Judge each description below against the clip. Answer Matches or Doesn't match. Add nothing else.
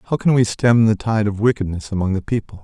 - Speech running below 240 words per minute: Doesn't match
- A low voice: Matches